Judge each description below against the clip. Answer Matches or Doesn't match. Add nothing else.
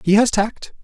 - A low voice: Doesn't match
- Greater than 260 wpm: Doesn't match